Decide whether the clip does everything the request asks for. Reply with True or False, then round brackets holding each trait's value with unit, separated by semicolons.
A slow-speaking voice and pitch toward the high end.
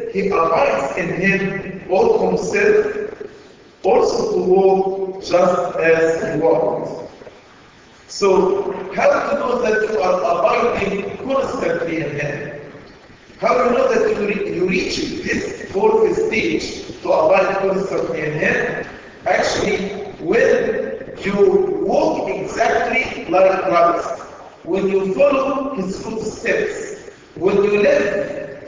True (120 wpm; 220 Hz)